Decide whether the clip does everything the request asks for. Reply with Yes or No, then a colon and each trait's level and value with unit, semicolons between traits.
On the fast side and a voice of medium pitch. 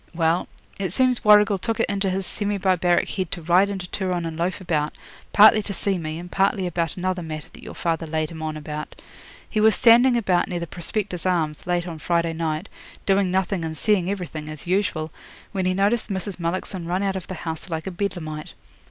Yes: fast, 210 wpm; medium, 180 Hz